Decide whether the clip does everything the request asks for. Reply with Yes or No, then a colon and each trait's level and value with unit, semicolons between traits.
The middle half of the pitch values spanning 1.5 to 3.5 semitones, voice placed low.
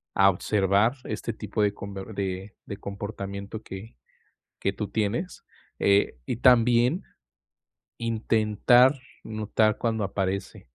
Yes: narrow, 2.4 semitones; low, 105 Hz